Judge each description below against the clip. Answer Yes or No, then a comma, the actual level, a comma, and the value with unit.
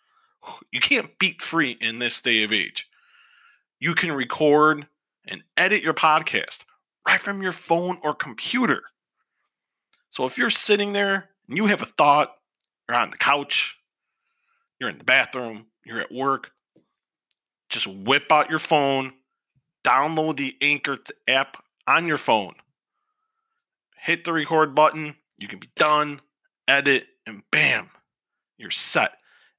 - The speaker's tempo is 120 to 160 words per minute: Yes, average, 140 wpm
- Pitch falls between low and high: Yes, medium, 155 Hz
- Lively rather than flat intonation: Yes, wide, 6.4 semitones